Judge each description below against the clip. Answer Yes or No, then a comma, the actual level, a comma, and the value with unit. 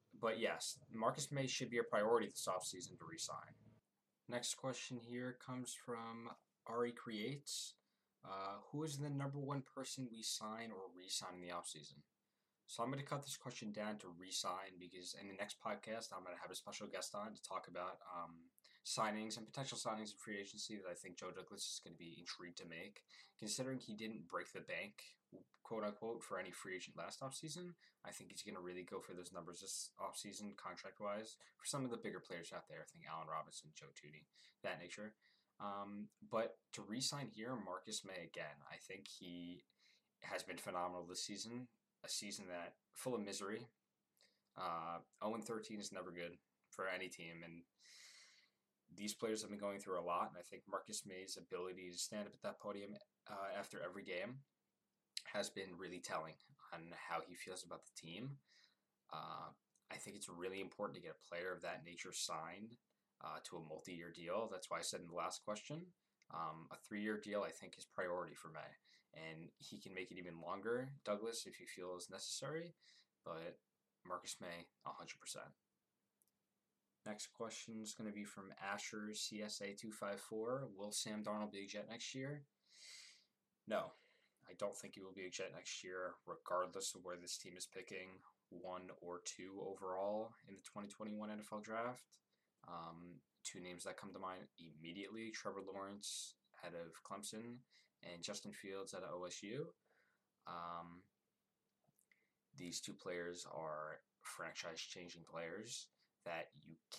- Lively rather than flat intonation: No, average, 4.3 semitones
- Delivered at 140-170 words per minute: No, average, 180 wpm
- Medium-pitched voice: No, low, 100 Hz